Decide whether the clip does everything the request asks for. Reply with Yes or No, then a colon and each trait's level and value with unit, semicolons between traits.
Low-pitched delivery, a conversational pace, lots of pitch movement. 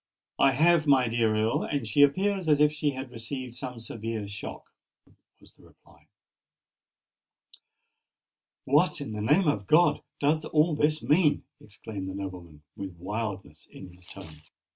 Yes: low, 115 Hz; average, 150 wpm; wide, 6.8 semitones